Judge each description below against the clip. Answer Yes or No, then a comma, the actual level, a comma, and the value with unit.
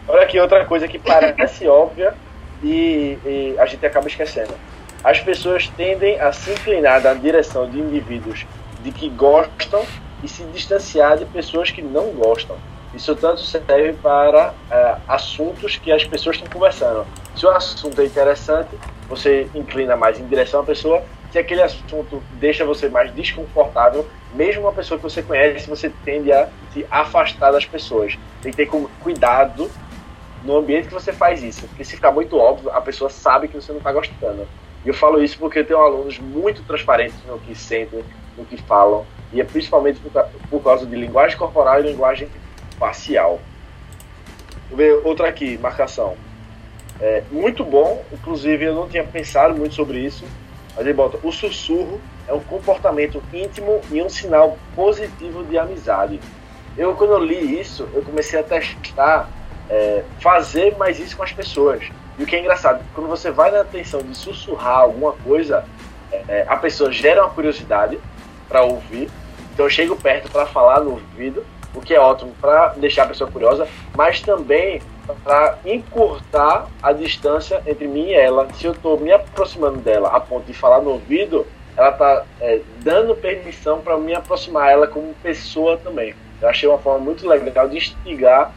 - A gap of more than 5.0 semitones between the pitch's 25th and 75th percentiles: Yes, wide, 5.5 semitones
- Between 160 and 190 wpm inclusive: Yes, average, 175 wpm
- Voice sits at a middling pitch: Yes, medium, 150 Hz